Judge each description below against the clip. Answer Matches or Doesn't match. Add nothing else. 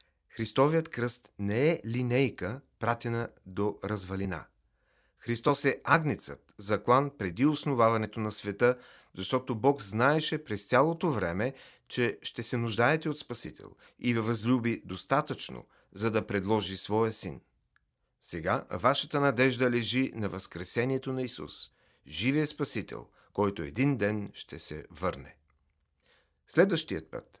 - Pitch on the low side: Matches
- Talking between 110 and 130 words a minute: Matches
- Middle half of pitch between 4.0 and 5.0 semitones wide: Matches